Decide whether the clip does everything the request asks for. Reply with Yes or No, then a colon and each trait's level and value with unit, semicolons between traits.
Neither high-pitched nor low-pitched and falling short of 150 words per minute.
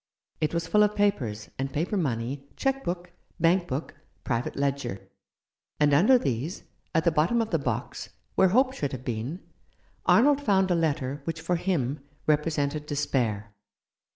No: medium, 155 Hz; average, 155 wpm